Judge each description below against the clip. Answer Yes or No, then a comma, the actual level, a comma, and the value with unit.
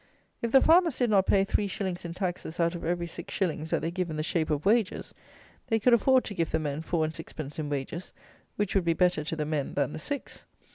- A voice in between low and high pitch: Yes, medium, 170 Hz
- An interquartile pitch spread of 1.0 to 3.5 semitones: No, average, 4.4 semitones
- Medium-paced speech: No, fast, 250 wpm